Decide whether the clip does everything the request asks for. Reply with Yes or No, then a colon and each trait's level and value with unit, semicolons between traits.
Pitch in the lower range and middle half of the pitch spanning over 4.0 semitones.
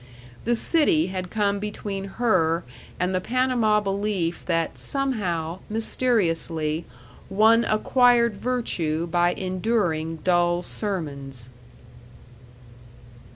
No: high, 190 Hz; average, 5.0 semitones